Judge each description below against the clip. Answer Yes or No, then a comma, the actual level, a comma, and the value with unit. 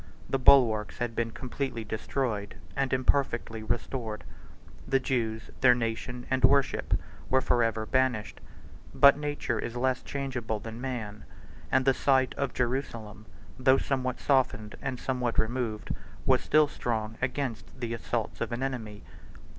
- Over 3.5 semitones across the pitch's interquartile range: No, average, 2.8 semitones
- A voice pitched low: Yes, low, 125 Hz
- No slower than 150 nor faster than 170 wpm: No, average, 140 wpm